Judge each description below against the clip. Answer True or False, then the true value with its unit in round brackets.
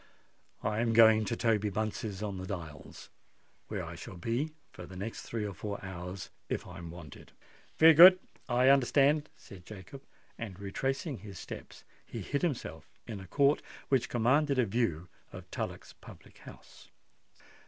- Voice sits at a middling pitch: False (110 Hz)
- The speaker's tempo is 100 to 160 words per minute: True (155 wpm)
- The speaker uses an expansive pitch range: True (6.0 semitones)